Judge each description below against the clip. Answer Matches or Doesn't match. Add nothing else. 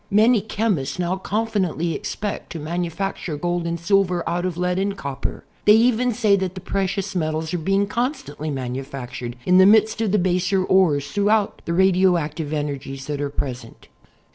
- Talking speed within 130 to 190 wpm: Matches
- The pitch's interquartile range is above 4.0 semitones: Matches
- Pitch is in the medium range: Matches